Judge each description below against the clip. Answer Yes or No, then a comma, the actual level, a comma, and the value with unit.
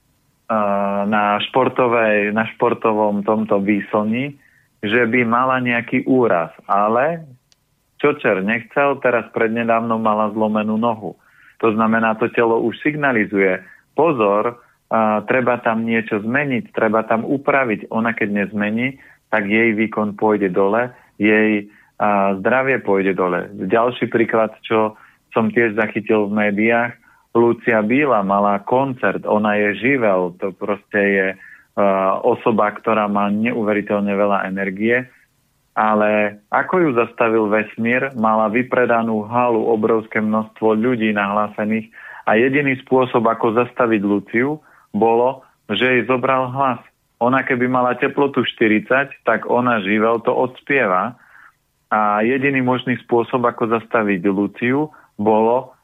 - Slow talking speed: No, average, 120 wpm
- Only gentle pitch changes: No, average, 3.0 semitones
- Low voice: Yes, low, 115 Hz